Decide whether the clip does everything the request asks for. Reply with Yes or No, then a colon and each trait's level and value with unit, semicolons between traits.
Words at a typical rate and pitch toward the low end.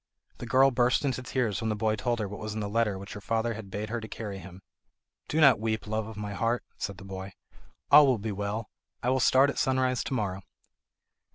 No: fast, 245 wpm; low, 110 Hz